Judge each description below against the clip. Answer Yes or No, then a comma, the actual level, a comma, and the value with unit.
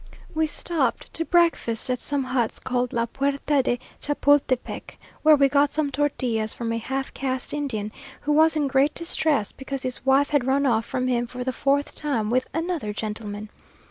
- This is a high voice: Yes, very high, 270 Hz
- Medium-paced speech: Yes, average, 175 wpm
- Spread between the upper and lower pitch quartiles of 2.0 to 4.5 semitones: Yes, average, 3.2 semitones